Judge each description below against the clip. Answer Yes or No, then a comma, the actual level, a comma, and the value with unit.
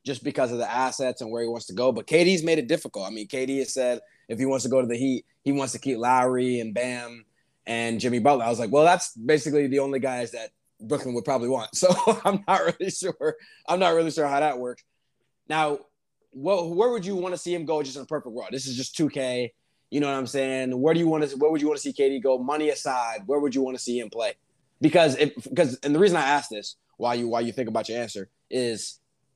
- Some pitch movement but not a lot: Yes, average, 3.7 semitones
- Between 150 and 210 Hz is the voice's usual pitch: No, low, 135 Hz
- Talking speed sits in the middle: No, fast, 265 wpm